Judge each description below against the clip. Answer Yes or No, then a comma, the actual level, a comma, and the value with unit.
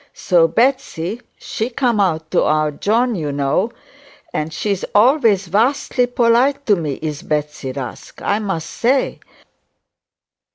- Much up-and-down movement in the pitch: Yes, wide, 7.6 semitones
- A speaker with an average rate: No, slow, 130 wpm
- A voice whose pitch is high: Yes, high, 200 Hz